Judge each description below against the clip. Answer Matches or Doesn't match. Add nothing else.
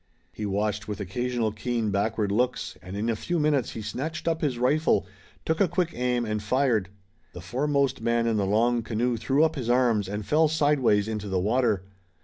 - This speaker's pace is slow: Doesn't match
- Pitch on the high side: Doesn't match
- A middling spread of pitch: Matches